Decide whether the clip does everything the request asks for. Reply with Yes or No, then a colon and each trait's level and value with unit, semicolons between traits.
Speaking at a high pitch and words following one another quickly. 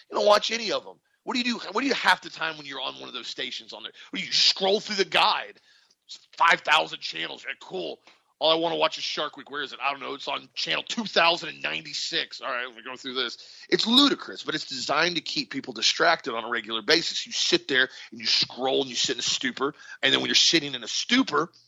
Yes: high, 210 Hz; fast, 255 wpm